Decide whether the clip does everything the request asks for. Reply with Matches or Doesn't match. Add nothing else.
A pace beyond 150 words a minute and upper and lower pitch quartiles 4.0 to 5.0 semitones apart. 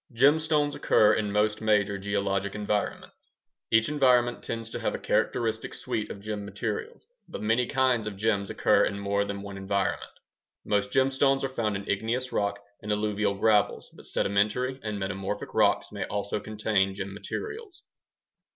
Doesn't match